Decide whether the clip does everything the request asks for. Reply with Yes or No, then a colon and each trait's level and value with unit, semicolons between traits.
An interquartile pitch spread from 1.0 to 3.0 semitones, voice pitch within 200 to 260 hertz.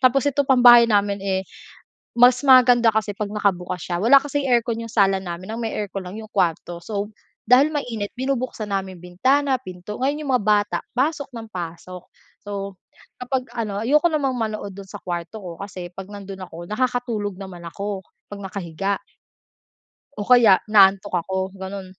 No: average, 4.5 semitones; high, 205 Hz